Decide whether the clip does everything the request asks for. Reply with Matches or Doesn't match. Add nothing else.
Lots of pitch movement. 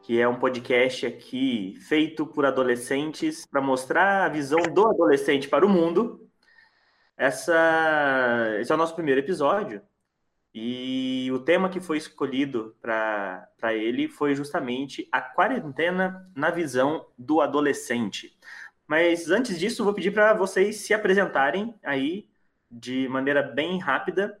Matches